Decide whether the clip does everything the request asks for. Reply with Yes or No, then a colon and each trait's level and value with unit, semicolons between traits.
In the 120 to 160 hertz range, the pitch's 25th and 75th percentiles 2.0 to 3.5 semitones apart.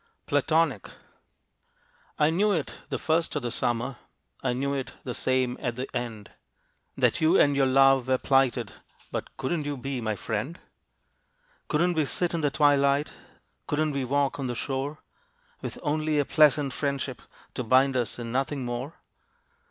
Yes: medium, 140 Hz; average, 2.8 semitones